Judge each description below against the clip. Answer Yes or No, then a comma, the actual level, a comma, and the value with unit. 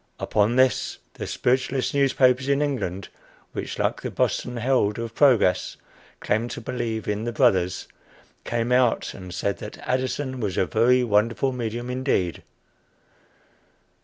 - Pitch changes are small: No, average, 3.6 semitones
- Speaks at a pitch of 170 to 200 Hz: No, low, 120 Hz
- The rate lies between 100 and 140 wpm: Yes, slow, 135 wpm